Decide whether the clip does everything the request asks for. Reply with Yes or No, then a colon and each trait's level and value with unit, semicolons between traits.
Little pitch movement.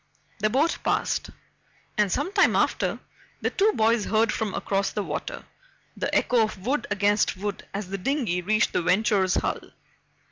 No: average, 3.2 semitones